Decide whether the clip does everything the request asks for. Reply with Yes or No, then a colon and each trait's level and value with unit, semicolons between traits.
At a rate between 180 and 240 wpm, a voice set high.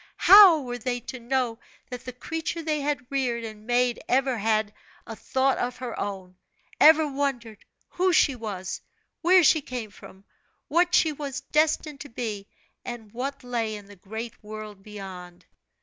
No: average, 165 wpm; high, 245 Hz